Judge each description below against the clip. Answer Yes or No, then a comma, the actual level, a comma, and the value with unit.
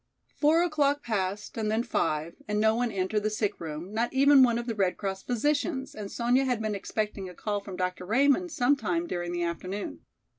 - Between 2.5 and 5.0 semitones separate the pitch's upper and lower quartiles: No, wide, 5.4 semitones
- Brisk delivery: Yes, fast, 210 wpm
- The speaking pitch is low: No, high, 215 Hz